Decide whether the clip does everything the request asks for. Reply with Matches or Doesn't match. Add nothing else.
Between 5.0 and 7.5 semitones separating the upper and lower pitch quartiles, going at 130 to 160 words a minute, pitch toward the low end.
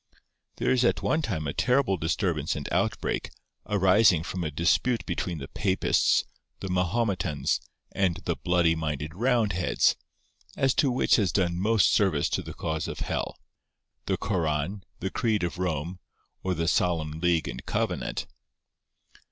Doesn't match